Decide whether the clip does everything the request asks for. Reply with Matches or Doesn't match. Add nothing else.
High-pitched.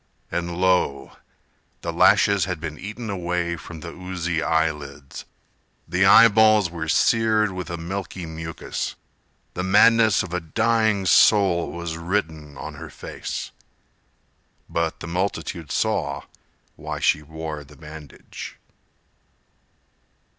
Doesn't match